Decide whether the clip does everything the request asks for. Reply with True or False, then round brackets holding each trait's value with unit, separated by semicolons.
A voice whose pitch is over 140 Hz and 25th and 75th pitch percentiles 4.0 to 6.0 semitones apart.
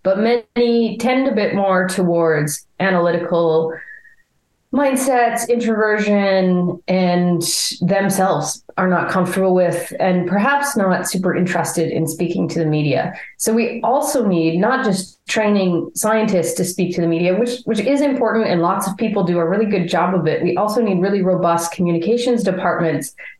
True (185 Hz; 4.4 semitones)